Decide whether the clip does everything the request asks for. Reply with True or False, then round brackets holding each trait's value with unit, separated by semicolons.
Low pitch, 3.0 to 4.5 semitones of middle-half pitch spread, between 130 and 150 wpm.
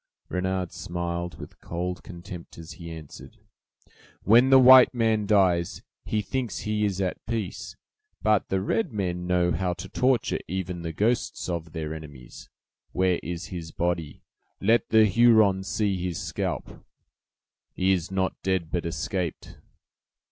True (90 Hz; 3.6 semitones; 145 wpm)